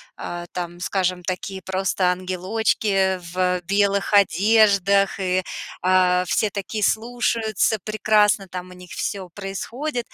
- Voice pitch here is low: No, high, 195 Hz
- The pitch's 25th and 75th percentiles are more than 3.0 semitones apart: No, narrow, 2.5 semitones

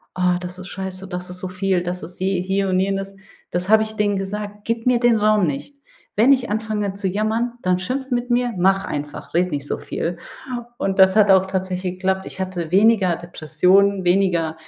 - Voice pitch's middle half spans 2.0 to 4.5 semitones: Yes, narrow, 2.5 semitones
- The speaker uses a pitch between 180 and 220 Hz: Yes, high, 190 Hz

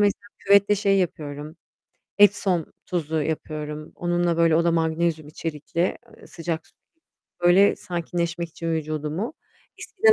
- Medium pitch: Yes, medium, 170 Hz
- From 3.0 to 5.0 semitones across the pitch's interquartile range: No, narrow, 2.5 semitones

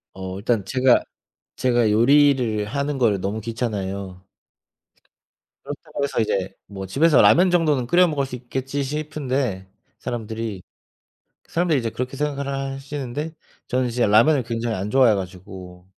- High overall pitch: No, low, 125 Hz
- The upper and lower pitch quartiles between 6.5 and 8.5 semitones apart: No, average, 5.1 semitones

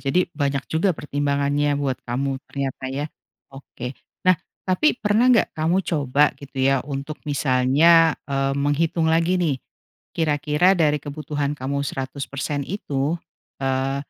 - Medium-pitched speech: Yes, medium, 145 Hz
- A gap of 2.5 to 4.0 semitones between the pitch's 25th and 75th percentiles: Yes, average, 2.8 semitones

